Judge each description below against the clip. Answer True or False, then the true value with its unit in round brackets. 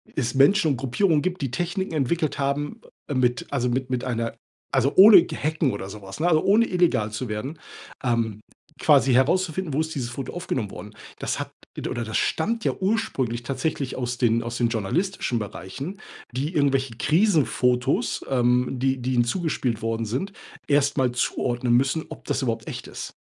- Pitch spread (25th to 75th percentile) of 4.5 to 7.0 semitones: True (4.8 semitones)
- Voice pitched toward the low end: True (130 Hz)